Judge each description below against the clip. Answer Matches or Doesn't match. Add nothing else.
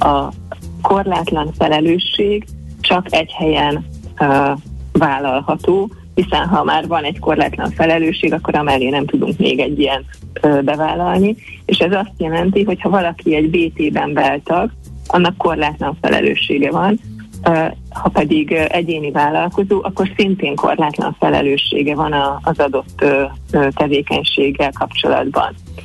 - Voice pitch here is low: Doesn't match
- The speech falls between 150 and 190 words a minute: Doesn't match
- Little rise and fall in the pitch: Doesn't match